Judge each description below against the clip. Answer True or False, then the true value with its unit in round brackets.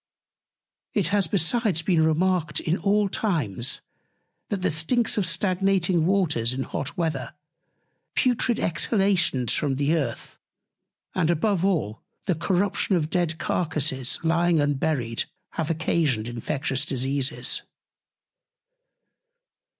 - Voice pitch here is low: False (165 Hz)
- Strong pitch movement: False (4.7 semitones)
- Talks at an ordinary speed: False (110 wpm)